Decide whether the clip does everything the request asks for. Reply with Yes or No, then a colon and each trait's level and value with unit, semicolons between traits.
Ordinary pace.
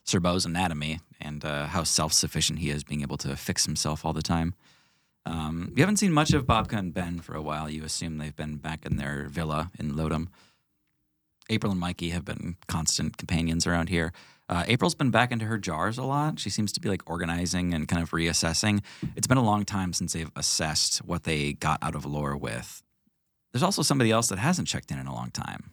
No: fast, 220 wpm